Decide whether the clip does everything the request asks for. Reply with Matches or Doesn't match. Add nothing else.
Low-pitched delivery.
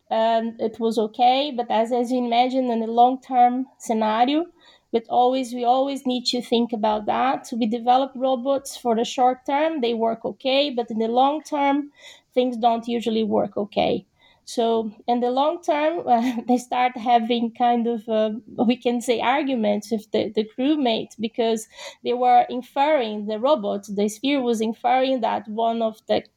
Doesn't match